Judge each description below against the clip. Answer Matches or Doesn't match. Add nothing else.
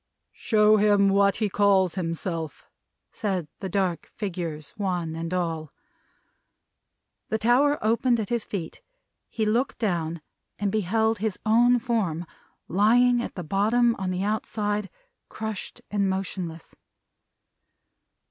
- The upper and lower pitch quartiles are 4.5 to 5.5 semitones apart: Doesn't match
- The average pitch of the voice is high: Matches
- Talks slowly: Matches